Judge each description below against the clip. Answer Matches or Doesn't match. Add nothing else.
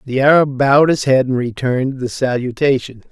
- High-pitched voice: Doesn't match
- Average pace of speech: Matches